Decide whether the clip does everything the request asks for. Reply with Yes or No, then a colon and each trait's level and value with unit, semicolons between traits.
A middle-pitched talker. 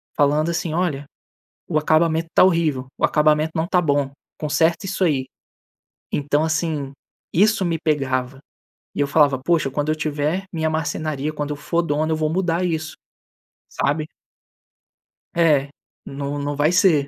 Yes: medium, 155 Hz